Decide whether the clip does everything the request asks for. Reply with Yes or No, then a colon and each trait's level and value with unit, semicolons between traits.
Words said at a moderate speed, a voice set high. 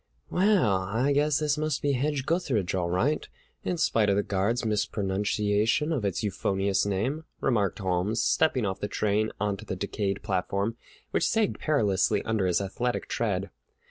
No: average, 160 wpm; low, 105 Hz